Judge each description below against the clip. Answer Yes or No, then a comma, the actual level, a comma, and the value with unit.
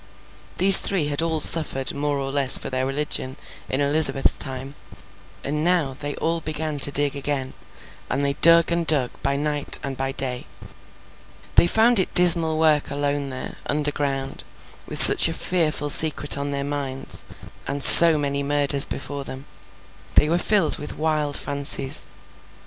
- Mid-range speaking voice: Yes, medium, 145 Hz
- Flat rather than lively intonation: Yes, narrow, 2.3 semitones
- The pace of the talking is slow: No, average, 160 wpm